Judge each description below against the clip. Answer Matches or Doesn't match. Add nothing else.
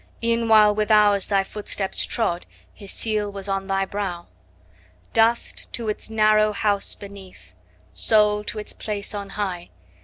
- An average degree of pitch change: Doesn't match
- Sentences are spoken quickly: Doesn't match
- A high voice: Matches